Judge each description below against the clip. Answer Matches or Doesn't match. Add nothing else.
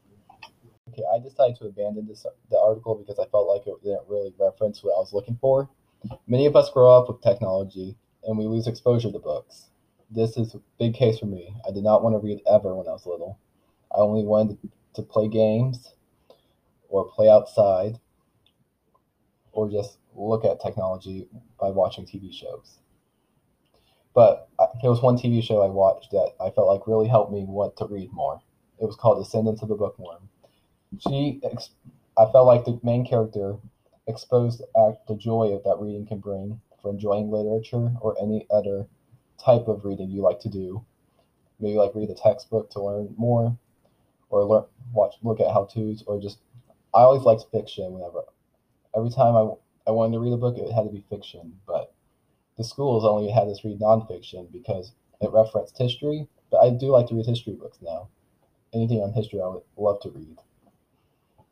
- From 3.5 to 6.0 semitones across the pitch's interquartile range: Doesn't match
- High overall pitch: Doesn't match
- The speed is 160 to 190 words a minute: Matches